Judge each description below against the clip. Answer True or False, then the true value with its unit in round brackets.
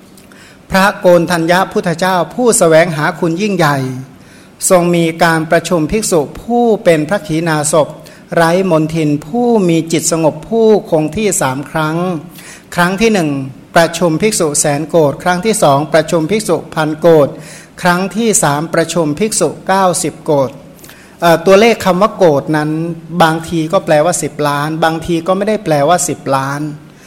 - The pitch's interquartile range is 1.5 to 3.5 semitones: True (3.1 semitones)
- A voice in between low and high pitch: True (165 Hz)